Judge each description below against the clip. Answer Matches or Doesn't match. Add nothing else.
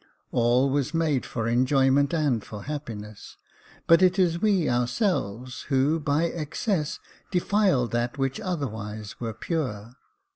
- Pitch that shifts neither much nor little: Doesn't match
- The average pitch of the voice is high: Doesn't match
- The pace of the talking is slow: Matches